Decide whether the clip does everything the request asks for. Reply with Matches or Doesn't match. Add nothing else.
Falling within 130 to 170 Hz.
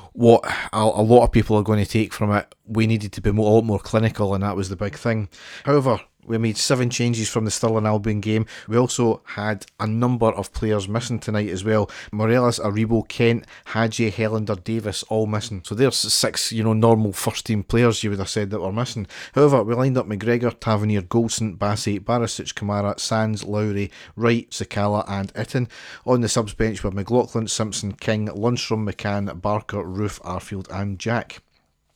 Doesn't match